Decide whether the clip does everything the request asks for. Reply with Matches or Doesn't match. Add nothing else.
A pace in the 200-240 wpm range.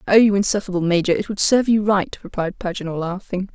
Matches